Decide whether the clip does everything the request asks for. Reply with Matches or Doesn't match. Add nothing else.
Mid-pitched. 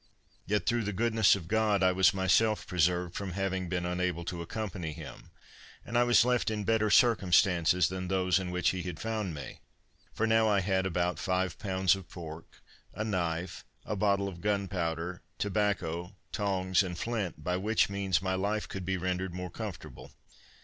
Doesn't match